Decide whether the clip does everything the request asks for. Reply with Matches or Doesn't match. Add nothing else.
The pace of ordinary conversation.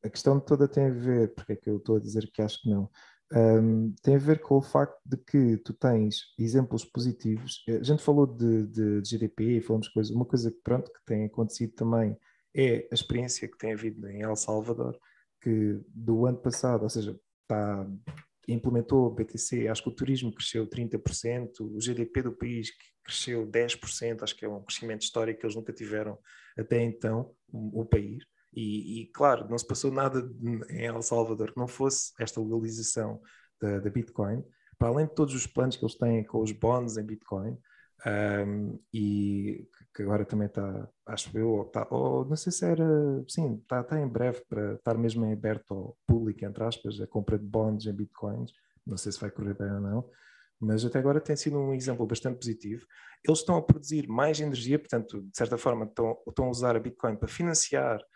Doesn't match